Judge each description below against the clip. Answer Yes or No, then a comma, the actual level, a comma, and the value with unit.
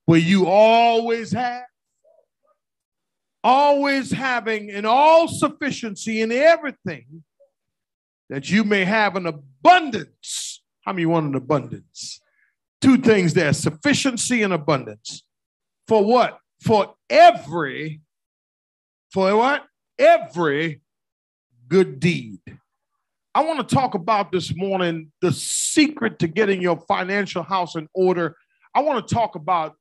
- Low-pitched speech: No, high, 200 Hz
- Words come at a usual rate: No, slow, 115 wpm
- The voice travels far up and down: Yes, wide, 7.3 semitones